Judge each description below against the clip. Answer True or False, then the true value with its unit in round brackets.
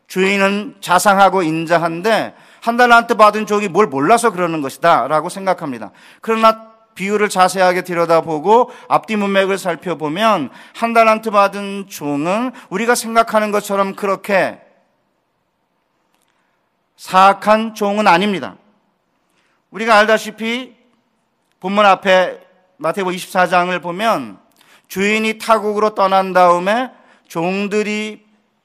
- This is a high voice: True (200 Hz)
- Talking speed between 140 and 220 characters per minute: False (260 characters per minute)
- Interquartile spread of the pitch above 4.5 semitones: False (3.4 semitones)